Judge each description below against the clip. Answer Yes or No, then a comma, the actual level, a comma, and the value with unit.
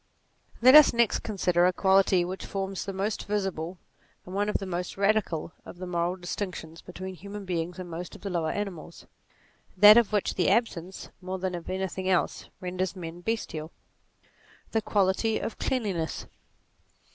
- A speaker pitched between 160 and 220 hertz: Yes, medium, 185 Hz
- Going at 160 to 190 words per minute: Yes, average, 170 wpm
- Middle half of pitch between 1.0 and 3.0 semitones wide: Yes, narrow, 2.5 semitones